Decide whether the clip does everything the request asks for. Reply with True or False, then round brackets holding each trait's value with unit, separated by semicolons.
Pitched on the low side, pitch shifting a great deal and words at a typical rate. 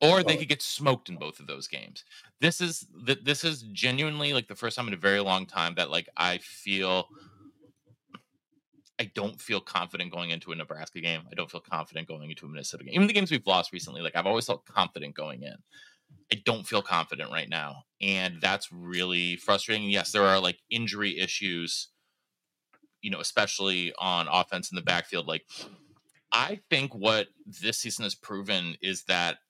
True (100 Hz; 7.3 semitones; 190 wpm)